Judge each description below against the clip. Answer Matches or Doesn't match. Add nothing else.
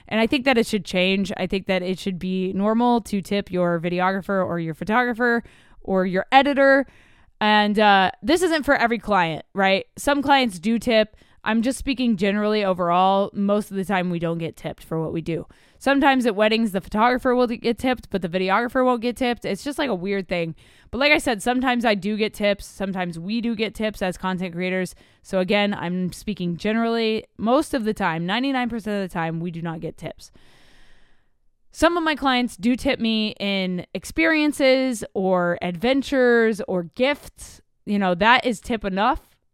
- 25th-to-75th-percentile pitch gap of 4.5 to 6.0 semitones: Matches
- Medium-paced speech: Matches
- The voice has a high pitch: Matches